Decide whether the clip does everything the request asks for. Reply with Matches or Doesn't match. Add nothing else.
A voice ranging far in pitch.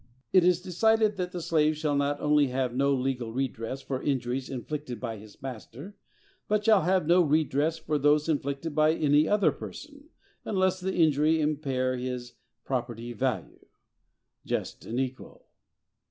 Doesn't match